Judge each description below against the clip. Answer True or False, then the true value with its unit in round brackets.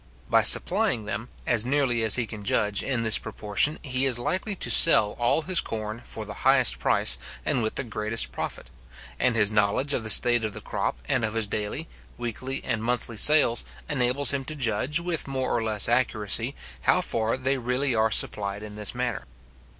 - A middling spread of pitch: True (3.5 semitones)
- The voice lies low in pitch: True (115 Hz)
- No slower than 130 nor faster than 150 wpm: False (195 wpm)